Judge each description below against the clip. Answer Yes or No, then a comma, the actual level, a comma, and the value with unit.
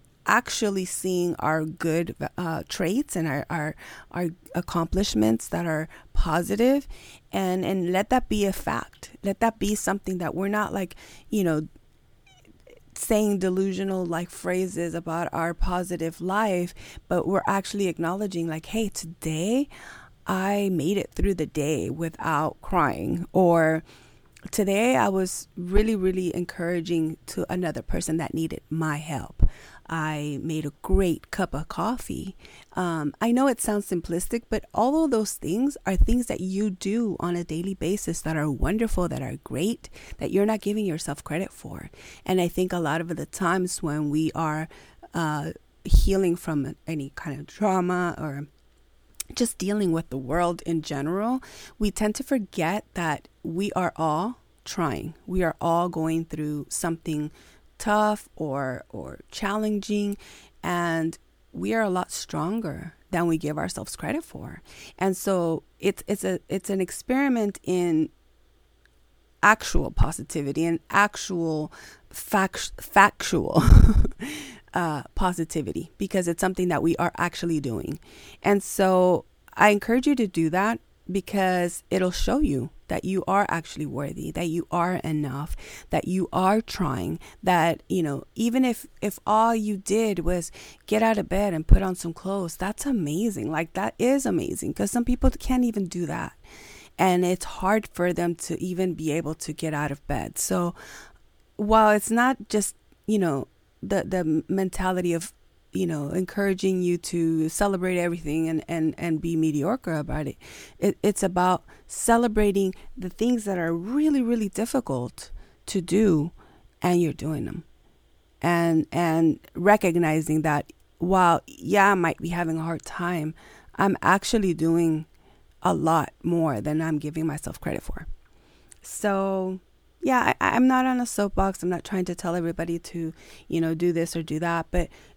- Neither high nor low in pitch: Yes, medium, 180 Hz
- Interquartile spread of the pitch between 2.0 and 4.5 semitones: Yes, average, 3.7 semitones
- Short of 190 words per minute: Yes, average, 155 wpm